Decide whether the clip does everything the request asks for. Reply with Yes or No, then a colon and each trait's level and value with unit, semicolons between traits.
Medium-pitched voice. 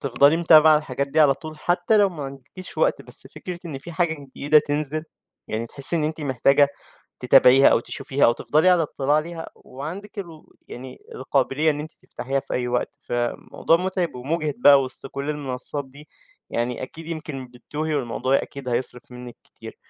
Yes: medium, 145 Hz